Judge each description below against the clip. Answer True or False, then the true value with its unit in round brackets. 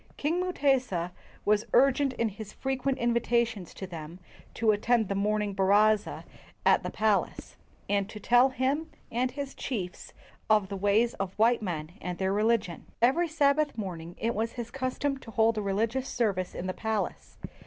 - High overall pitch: True (220 Hz)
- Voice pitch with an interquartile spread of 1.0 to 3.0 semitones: False (4.4 semitones)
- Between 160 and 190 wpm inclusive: True (165 wpm)